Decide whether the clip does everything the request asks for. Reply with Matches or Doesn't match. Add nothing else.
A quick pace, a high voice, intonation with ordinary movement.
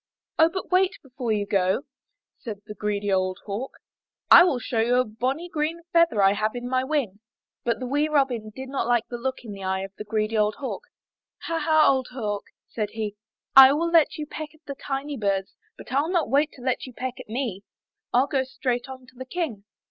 Matches